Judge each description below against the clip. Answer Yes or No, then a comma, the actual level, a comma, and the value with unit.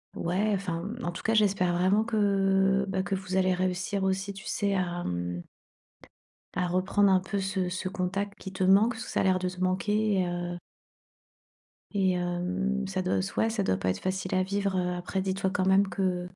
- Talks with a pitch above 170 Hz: Yes, high, 190 Hz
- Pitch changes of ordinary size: No, narrow, 1.5 semitones